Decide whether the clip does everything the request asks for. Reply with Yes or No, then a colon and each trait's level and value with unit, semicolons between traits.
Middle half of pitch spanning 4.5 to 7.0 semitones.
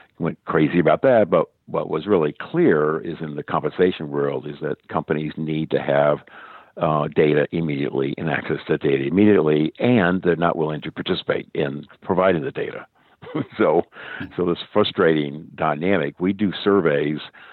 No: narrow, 2.6 semitones